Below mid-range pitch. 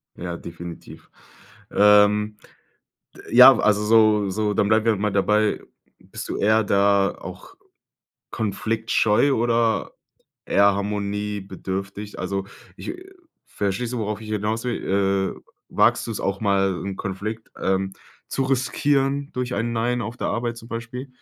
Yes: low, 105 Hz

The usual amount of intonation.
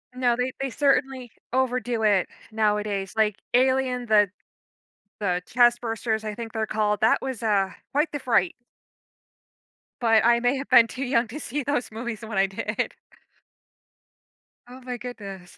Yes: average, 3.0 semitones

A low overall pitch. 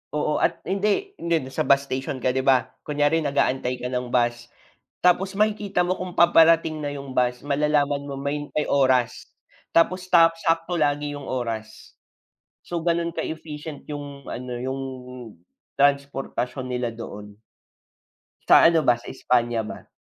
No: medium, 145 Hz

